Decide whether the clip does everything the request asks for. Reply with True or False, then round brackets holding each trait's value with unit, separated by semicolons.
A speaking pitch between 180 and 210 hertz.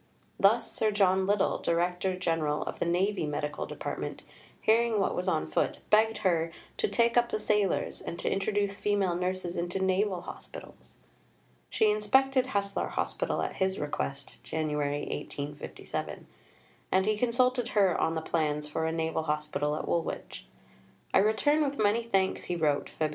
True (190 Hz)